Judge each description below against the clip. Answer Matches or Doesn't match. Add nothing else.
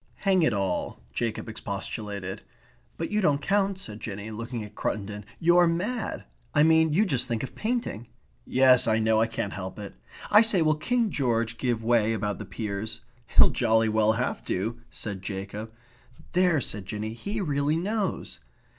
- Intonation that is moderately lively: Doesn't match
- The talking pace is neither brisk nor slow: Matches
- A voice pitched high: Doesn't match